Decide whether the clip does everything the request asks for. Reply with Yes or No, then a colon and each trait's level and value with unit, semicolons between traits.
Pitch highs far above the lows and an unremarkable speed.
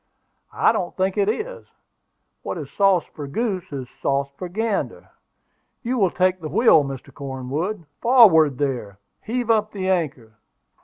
Yes: wide, 7.3 semitones; average, 150 wpm